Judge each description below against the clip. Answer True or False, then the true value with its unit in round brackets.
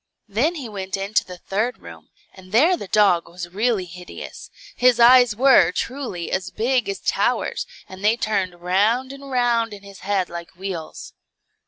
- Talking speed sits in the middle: True (170 wpm)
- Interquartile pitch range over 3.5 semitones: True (4.8 semitones)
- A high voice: True (205 Hz)